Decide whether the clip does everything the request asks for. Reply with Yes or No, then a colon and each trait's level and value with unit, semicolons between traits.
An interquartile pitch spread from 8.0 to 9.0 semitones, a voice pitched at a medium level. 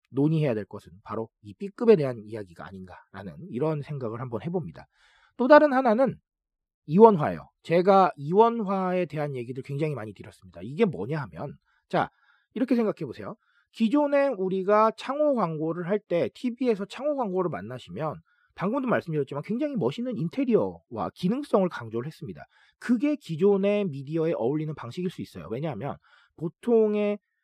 Yes: wide, 8.3 semitones; medium, 180 Hz